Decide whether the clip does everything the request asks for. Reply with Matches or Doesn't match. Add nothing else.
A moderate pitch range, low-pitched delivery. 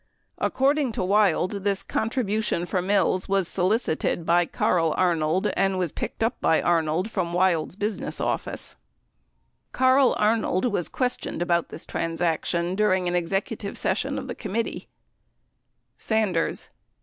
Doesn't match